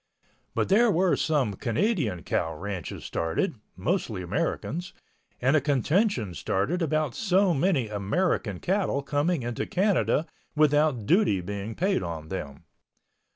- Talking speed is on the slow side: Yes, slow, 125 wpm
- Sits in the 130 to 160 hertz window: Yes, medium, 140 Hz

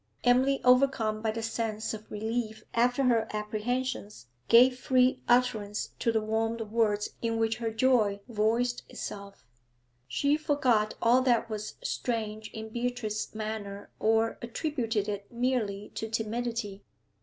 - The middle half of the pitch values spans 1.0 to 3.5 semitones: Yes, narrow, 2.4 semitones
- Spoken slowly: Yes, slow, 130 wpm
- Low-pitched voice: No, high, 225 Hz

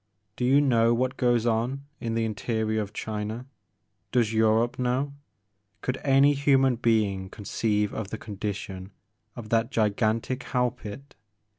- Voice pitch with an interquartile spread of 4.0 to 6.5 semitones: No, average, 2.8 semitones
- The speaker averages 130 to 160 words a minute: Yes, average, 145 wpm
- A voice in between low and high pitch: No, low, 115 Hz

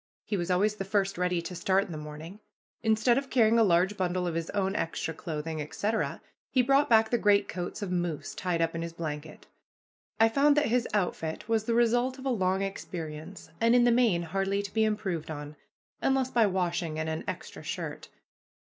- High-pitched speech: Yes, high, 195 Hz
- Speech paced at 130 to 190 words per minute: No, average, 200 wpm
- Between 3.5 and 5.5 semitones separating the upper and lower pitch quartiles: Yes, average, 5.0 semitones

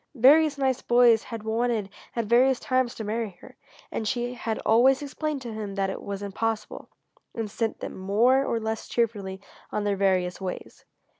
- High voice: Yes, high, 225 Hz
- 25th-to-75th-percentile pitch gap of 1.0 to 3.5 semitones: Yes, average, 3.2 semitones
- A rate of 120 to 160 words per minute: No, average, 175 wpm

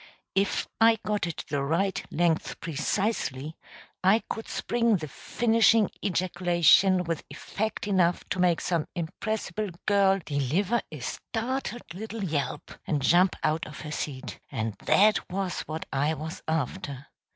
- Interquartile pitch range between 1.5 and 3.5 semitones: No, average, 5.1 semitones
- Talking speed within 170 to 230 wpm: No, average, 140 wpm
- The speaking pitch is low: No, medium, 175 Hz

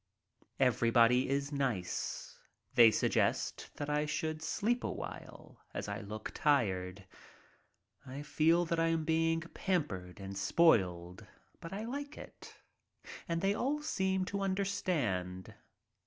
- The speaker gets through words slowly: Yes, slow, 125 wpm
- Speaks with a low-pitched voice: No, medium, 150 Hz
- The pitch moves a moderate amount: No, wide, 8.4 semitones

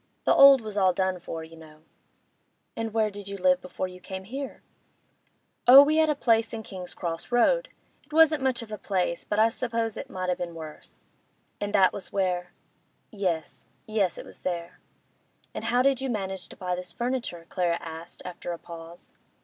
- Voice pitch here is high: Yes, high, 195 Hz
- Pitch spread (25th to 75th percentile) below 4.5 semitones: No, average, 5.1 semitones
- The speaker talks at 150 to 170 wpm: No, average, 185 wpm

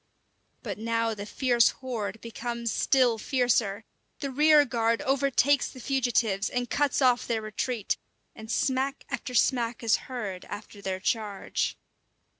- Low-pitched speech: No, high, 235 Hz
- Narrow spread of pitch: No, average, 3.0 semitones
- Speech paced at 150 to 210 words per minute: No, slow, 135 wpm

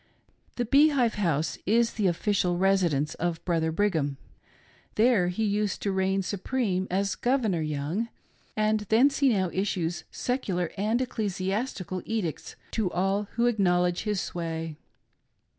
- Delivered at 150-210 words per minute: No, slow, 135 wpm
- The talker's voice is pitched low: No, high, 195 Hz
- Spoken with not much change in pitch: No, average, 3.9 semitones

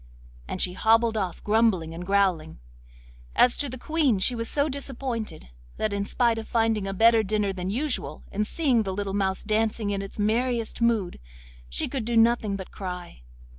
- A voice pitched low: No, high, 215 Hz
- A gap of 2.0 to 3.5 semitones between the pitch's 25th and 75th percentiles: Yes, average, 3.2 semitones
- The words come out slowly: No, average, 180 wpm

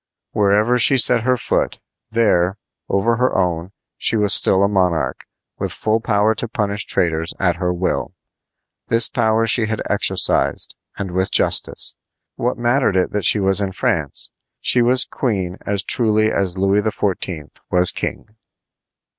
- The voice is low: Yes, low, 105 Hz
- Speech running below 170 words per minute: Yes, average, 155 wpm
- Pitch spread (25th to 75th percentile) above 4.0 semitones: No, average, 3.5 semitones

